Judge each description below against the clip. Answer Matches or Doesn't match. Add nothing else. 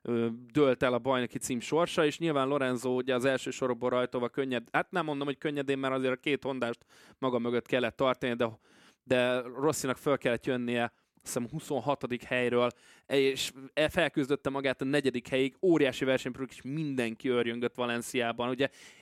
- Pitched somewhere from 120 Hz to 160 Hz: Matches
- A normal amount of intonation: Doesn't match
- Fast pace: Matches